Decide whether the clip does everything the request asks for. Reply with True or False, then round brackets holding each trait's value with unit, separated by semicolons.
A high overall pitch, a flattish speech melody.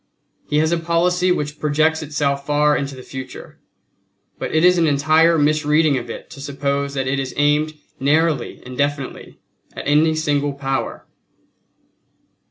False (145 Hz; 2.0 semitones)